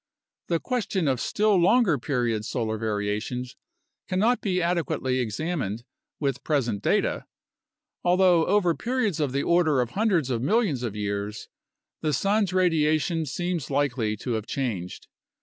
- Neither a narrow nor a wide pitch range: No, wide, 7.3 semitones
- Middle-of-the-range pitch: Yes, medium, 150 Hz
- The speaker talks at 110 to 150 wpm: Yes, slow, 135 wpm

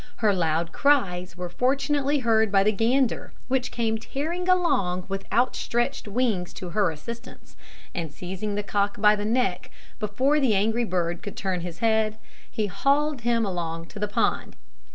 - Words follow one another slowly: No, average, 165 wpm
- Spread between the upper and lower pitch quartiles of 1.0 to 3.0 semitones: No, average, 5.3 semitones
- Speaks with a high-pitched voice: Yes, high, 210 Hz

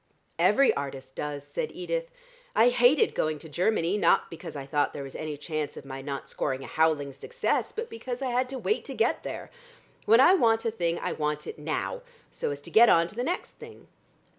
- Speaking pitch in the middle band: Yes, medium, 165 Hz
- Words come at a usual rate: No, fast, 215 wpm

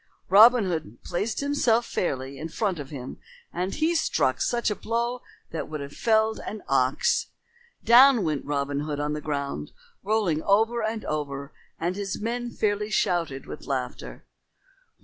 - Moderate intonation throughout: No, wide, 7.6 semitones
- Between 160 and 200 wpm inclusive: No, average, 150 wpm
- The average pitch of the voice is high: No, medium, 180 Hz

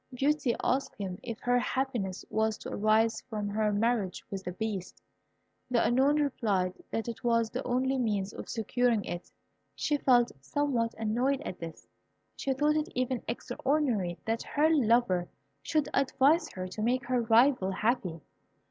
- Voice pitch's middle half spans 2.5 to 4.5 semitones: Yes, average, 4.0 semitones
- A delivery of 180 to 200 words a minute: No, average, 155 wpm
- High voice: Yes, high, 235 Hz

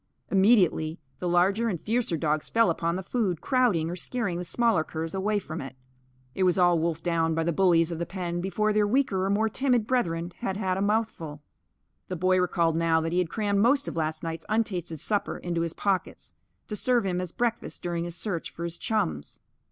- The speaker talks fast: Yes, fast, 210 wpm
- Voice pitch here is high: No, medium, 180 Hz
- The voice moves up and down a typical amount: Yes, average, 4.1 semitones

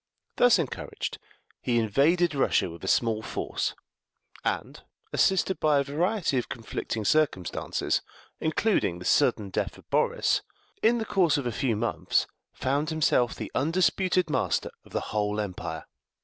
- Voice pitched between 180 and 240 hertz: No, medium, 140 Hz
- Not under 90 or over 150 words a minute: Yes, average, 145 wpm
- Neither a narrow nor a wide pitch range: No, wide, 7.9 semitones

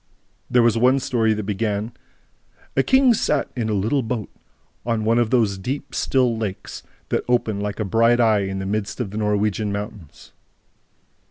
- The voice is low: Yes, low, 110 Hz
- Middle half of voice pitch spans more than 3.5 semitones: No, average, 2.8 semitones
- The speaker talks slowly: No, average, 175 wpm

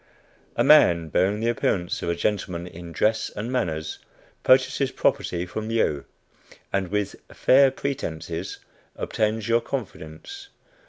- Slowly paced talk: Yes, slow, 125 wpm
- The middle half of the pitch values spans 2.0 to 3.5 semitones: No, wide, 5.4 semitones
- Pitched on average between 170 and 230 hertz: No, low, 105 Hz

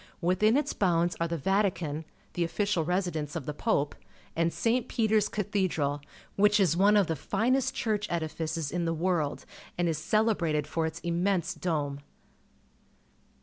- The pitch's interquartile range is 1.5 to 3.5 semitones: No, average, 4.4 semitones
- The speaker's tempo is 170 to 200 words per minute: No, average, 150 wpm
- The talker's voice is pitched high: No, medium, 175 Hz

